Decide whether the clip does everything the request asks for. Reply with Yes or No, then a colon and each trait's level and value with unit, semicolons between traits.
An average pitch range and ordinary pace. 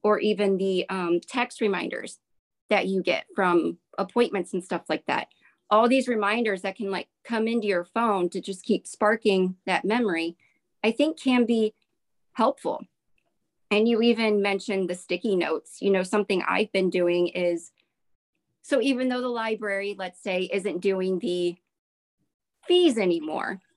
Yes: average, 3.3 semitones; average, 155 wpm